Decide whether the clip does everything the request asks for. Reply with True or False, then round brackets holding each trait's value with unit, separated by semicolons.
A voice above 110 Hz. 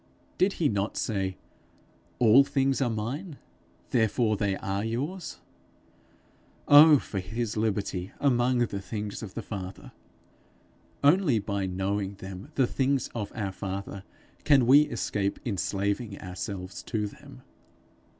False (105 Hz)